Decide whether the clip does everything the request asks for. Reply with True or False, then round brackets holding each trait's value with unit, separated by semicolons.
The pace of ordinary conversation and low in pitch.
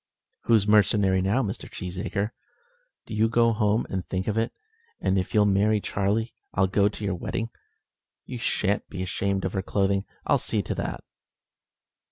True (170 wpm; 100 Hz)